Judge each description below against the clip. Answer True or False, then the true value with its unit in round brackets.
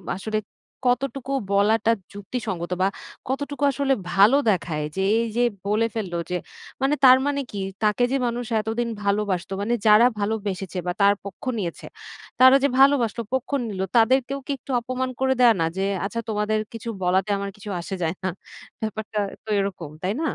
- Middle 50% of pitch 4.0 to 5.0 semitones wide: True (4.3 semitones)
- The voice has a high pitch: True (215 Hz)